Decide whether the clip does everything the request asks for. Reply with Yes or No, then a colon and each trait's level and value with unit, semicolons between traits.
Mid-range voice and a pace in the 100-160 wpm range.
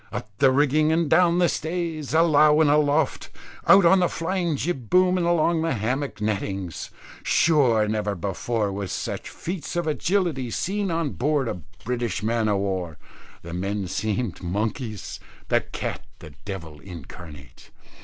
No: low, 130 Hz; average, 155 wpm